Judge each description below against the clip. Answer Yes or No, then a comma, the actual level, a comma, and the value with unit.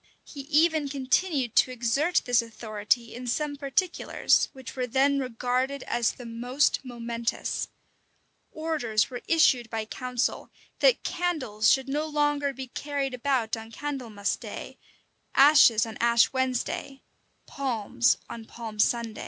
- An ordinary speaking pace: No, slow, 130 wpm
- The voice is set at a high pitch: Yes, very high, 255 Hz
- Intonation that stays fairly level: No, average, 3.5 semitones